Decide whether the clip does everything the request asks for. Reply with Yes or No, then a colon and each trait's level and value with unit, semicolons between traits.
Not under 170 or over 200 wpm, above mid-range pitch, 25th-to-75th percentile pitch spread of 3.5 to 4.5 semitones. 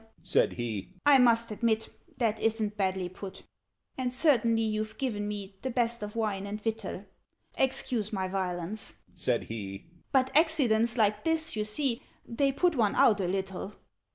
No: average, 155 wpm; high, 215 Hz; average, 3.8 semitones